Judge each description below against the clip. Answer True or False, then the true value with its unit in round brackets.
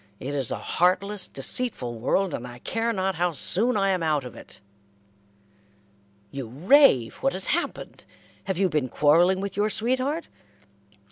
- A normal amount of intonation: False (6.6 semitones)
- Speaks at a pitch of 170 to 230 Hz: True (185 Hz)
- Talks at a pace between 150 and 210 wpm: True (155 wpm)